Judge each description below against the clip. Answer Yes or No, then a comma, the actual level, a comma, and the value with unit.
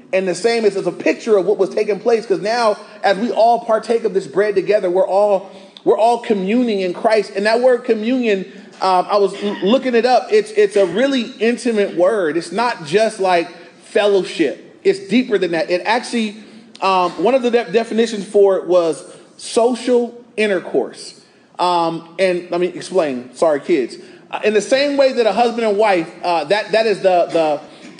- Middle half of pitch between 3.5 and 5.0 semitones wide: Yes, average, 3.8 semitones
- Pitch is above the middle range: Yes, high, 210 Hz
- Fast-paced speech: No, average, 195 wpm